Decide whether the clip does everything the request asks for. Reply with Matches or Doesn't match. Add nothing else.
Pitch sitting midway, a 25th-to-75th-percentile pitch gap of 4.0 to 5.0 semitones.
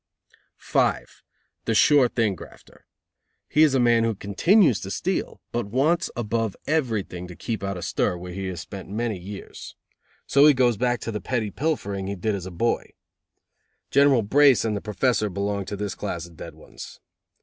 Doesn't match